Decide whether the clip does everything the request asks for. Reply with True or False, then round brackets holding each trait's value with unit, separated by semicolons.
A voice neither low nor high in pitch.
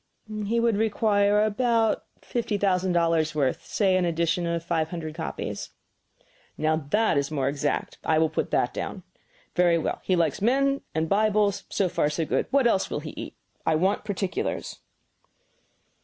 True (180 Hz)